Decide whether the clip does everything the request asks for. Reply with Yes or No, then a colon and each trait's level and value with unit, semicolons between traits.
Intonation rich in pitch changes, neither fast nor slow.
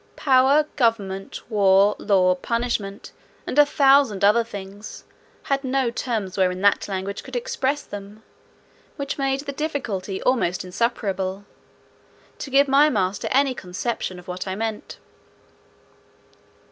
No: wide, 5.8 semitones; slow, 125 wpm